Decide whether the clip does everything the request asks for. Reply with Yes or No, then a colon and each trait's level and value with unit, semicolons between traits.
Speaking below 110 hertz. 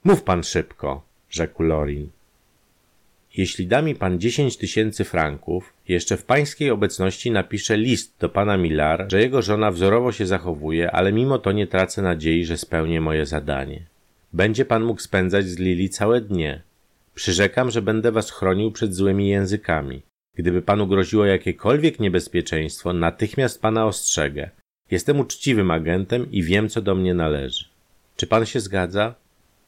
Yes: very low, 95 Hz